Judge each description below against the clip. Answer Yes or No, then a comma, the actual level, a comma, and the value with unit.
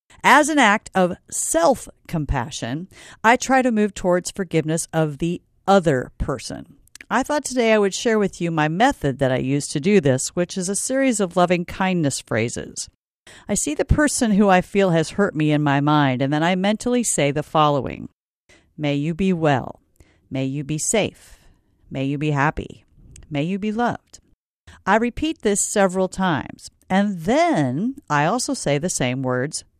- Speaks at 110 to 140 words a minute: No, average, 180 wpm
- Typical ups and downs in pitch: No, wide, 6.1 semitones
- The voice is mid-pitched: Yes, medium, 180 Hz